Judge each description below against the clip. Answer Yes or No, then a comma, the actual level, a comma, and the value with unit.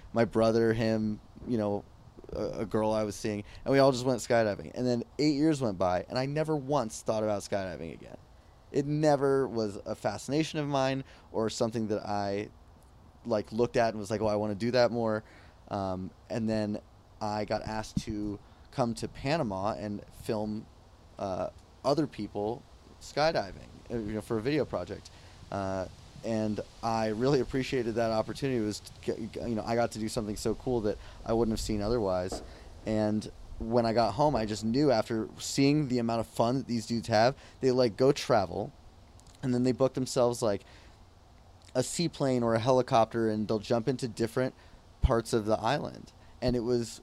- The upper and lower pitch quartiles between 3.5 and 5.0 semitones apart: No, average, 3.0 semitones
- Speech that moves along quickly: No, average, 190 wpm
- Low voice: Yes, low, 110 Hz